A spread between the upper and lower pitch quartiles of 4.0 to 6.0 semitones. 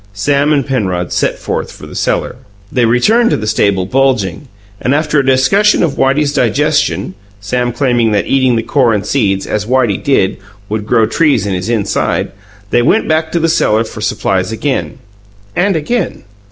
Yes: wide, 5.5 semitones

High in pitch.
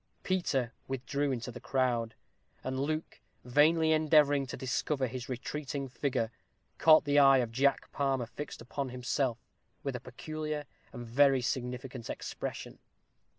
No: low, 135 Hz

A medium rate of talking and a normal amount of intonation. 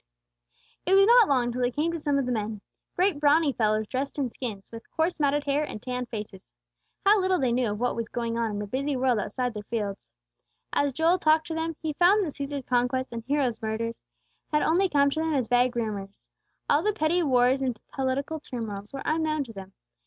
No: fast, 220 wpm; average, 5.0 semitones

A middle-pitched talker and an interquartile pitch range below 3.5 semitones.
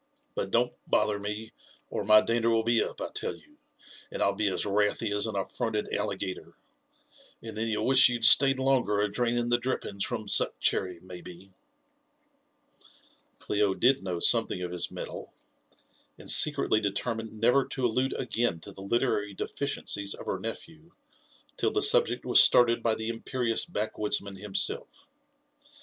No: low, 110 Hz; average, 3.1 semitones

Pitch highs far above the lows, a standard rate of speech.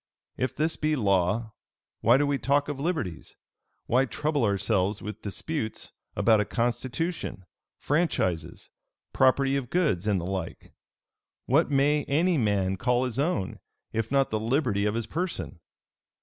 Yes: wide, 6.1 semitones; average, 145 wpm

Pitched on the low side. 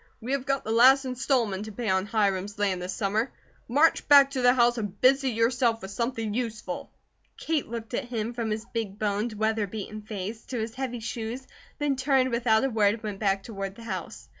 No: high, 225 Hz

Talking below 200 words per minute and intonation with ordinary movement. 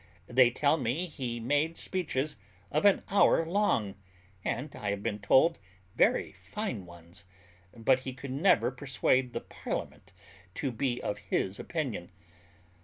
No: average, 140 wpm; wide, 6.1 semitones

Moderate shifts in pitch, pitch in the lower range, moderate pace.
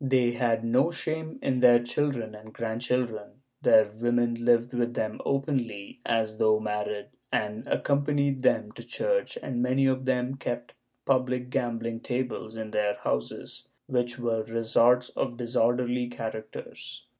No: narrow, 2.3 semitones; low, 120 Hz; average, 145 wpm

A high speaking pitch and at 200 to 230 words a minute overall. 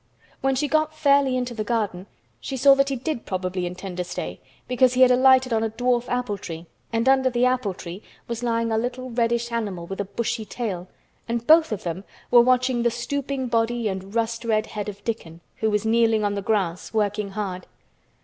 Yes: high, 230 Hz; fast, 205 wpm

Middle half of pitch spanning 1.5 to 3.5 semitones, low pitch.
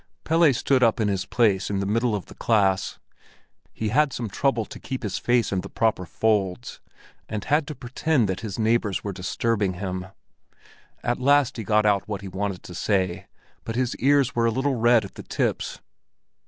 No: average, 3.9 semitones; low, 110 Hz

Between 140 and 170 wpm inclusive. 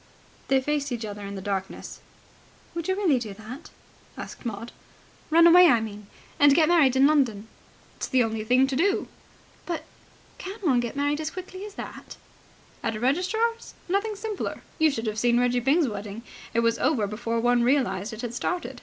No: average, 190 wpm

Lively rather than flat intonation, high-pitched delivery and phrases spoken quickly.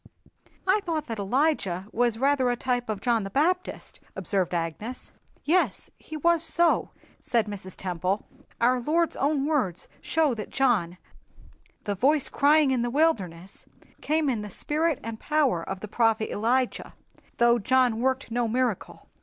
No: wide, 6.1 semitones; high, 245 Hz; average, 155 wpm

